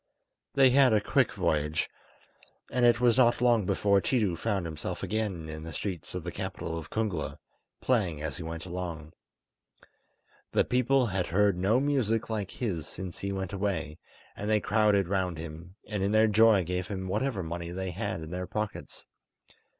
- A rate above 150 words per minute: Yes, average, 175 wpm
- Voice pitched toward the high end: No, very low, 95 Hz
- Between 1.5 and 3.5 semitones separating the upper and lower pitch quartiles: No, average, 4.4 semitones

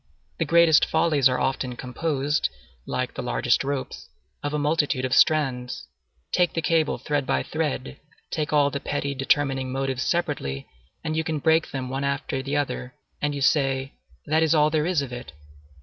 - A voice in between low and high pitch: Yes, medium, 145 Hz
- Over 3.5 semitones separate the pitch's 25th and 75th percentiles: No, average, 2.7 semitones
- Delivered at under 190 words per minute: Yes, average, 180 wpm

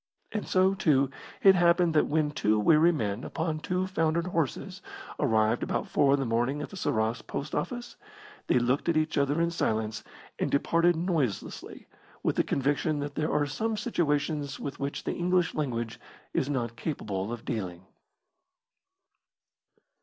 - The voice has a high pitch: No, medium, 145 Hz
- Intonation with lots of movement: Yes, wide, 5.9 semitones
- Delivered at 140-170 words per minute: Yes, average, 160 wpm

